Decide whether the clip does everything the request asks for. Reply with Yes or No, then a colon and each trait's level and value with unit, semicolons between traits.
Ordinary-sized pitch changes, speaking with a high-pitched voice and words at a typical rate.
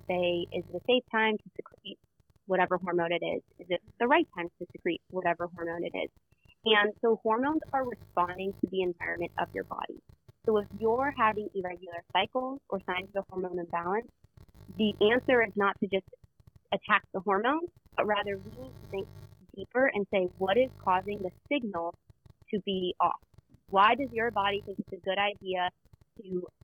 Yes: average, 3.7 semitones; high, 195 Hz; average, 180 wpm